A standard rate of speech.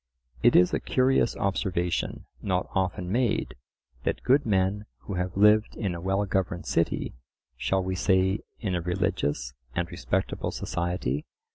Yes: average, 145 wpm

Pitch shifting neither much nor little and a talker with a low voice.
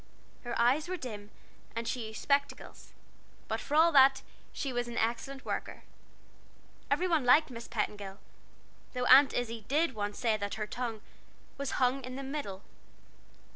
No: average, 3.8 semitones; high, 245 Hz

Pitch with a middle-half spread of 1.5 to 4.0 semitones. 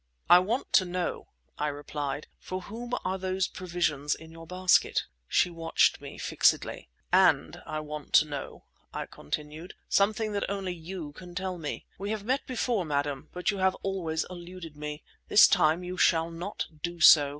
Yes: average, 3.6 semitones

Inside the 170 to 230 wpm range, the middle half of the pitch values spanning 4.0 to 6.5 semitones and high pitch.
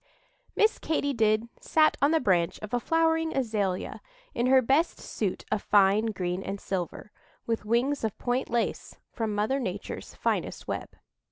No: average, 160 wpm; average, 5.1 semitones; high, 225 Hz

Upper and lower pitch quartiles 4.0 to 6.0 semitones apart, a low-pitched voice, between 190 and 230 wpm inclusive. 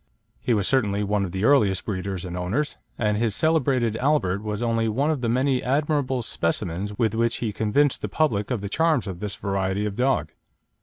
Yes: average, 4.9 semitones; low, 110 Hz; average, 200 wpm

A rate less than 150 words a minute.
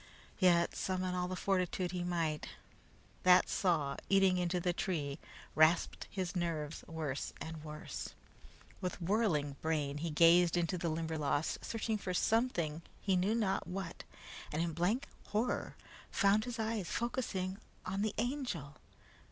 Yes: average, 140 wpm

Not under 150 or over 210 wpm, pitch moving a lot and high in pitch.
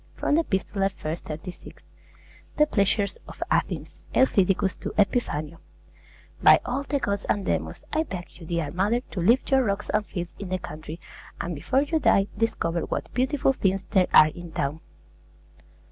Yes: average, 165 wpm; wide, 6.0 semitones; high, 195 Hz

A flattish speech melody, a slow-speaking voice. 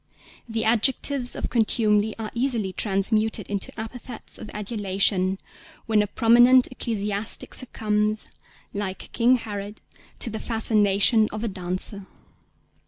Yes: narrow, 2.3 semitones; slow, 115 wpm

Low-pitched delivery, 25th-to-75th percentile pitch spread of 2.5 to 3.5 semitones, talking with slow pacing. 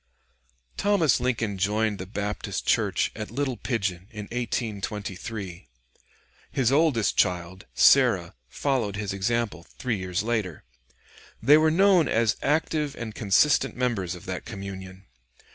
No: low, 110 Hz; average, 4.8 semitones; slow, 125 wpm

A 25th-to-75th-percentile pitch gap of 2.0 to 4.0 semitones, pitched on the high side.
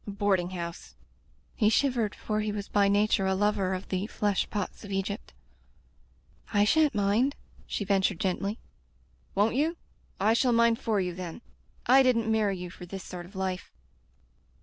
Yes: average, 2.7 semitones; high, 205 Hz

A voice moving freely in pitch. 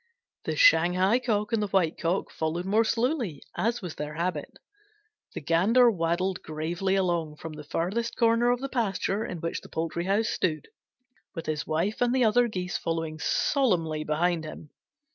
Yes: wide, 5.7 semitones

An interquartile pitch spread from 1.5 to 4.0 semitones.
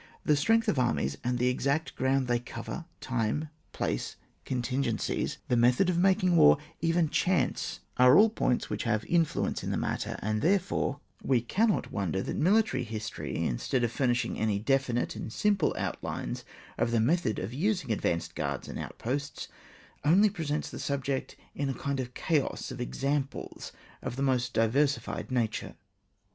No: average, 5.2 semitones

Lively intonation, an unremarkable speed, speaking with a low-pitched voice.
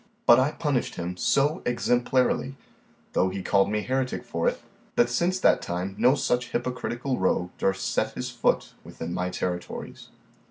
Yes: wide, 5.7 semitones; average, 160 wpm; low, 120 Hz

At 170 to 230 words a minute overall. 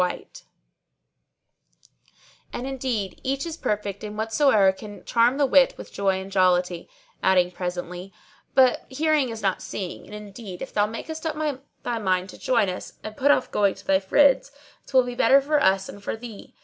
Yes: average, 175 wpm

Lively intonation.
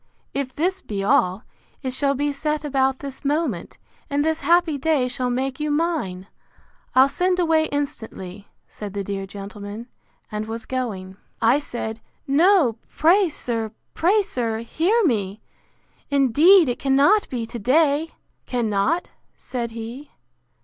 Yes: wide, 5.8 semitones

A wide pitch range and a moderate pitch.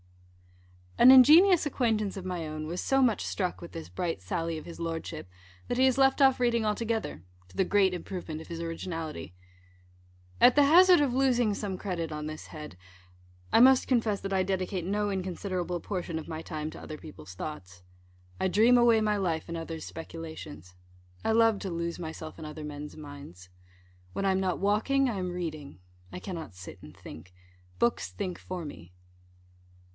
Yes: wide, 5.8 semitones; medium, 180 Hz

